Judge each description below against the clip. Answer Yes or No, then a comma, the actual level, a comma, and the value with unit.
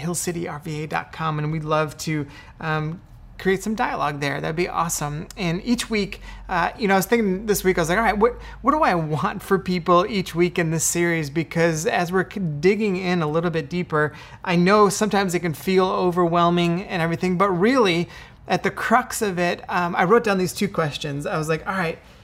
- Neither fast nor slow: No, fast, 210 wpm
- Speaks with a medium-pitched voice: Yes, medium, 175 Hz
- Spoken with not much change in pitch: No, average, 3.2 semitones